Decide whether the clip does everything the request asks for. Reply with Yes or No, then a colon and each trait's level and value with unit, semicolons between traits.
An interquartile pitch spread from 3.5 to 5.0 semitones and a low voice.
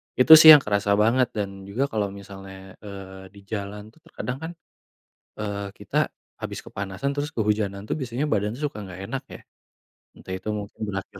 Yes: average, 4.1 semitones; low, 105 Hz